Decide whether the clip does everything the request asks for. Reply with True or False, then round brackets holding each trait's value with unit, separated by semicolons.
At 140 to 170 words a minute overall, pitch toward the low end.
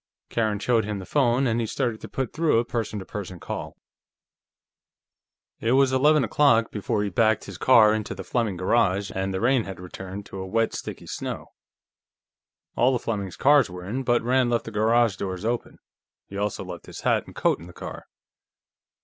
False (195 wpm; 110 Hz)